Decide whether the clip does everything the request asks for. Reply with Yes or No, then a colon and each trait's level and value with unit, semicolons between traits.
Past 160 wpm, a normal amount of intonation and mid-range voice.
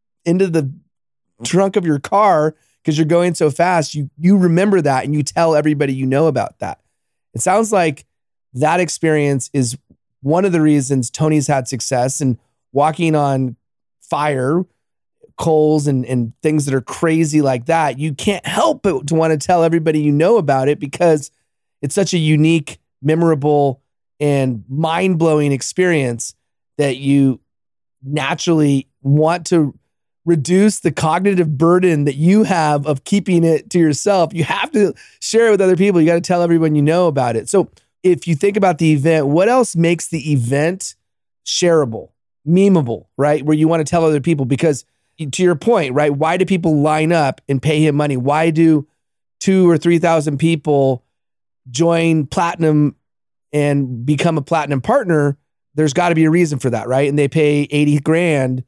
Yes: average, 170 wpm; average, 3.4 semitones; medium, 155 Hz